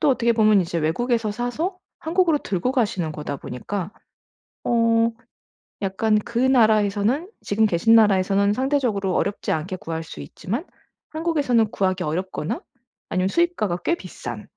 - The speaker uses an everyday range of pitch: Yes, average, 4.7 semitones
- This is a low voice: No, high, 215 Hz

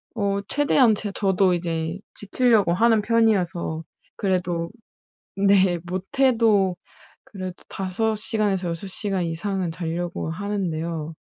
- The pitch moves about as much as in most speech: Yes, average, 3.3 semitones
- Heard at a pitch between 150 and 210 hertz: Yes, high, 190 Hz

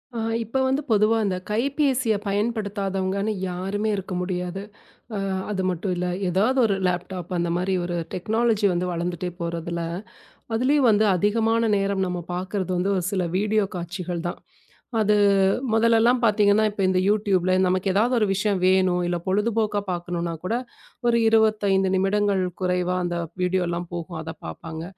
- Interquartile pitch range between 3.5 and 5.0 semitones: No, average, 3.1 semitones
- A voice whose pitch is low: No, high, 195 Hz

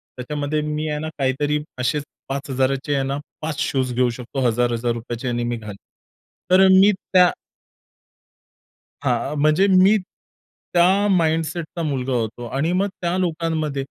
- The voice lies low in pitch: No, medium, 145 Hz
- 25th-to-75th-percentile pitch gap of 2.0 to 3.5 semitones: No, average, 4.4 semitones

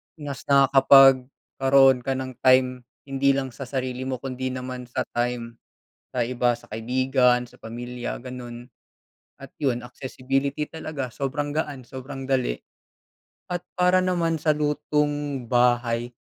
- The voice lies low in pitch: Yes, low, 130 Hz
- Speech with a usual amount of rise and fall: No, narrow, 2.1 semitones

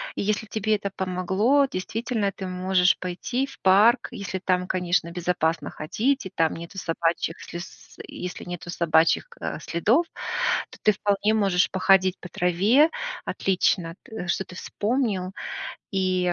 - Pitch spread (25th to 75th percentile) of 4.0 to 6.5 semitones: No, average, 3.1 semitones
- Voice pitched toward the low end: No, medium, 185 Hz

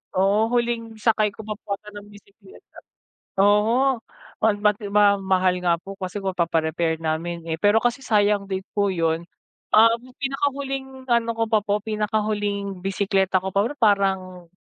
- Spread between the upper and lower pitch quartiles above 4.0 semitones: No, average, 2.8 semitones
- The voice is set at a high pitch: Yes, high, 205 Hz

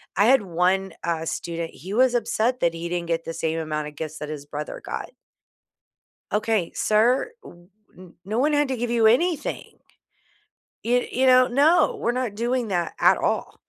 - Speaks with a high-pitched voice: Yes, high, 210 Hz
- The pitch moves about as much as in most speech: No, wide, 7.0 semitones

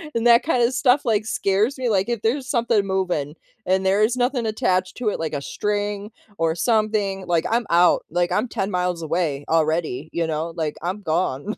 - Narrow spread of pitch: No, average, 5.0 semitones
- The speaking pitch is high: Yes, high, 195 Hz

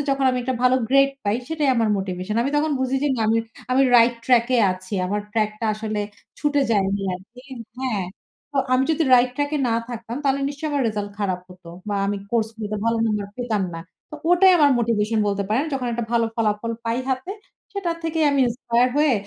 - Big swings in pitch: No, average, 4.4 semitones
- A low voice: No, high, 235 Hz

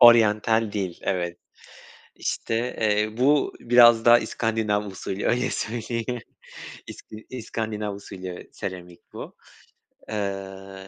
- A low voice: Yes, low, 105 Hz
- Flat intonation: No, average, 3.1 semitones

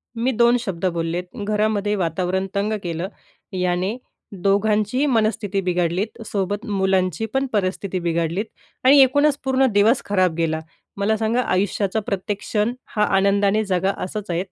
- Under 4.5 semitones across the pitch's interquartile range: Yes, average, 3.0 semitones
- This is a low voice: No, high, 200 Hz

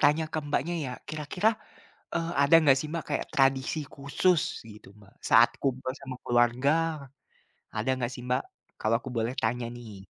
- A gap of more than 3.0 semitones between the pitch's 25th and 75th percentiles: Yes, average, 3.7 semitones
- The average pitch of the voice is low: Yes, low, 130 Hz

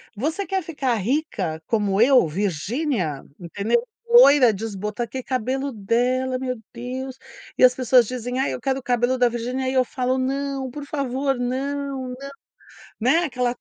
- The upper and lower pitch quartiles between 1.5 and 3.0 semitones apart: Yes, narrow, 2.6 semitones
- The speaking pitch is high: Yes, very high, 255 Hz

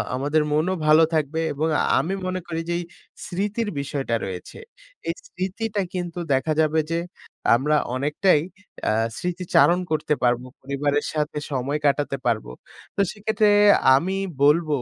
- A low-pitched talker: No, medium, 155 Hz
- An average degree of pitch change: Yes, average, 4.3 semitones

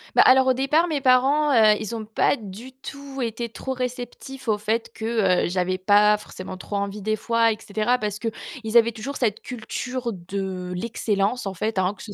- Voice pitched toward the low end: No, high, 225 Hz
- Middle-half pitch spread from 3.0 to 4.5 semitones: Yes, average, 3.7 semitones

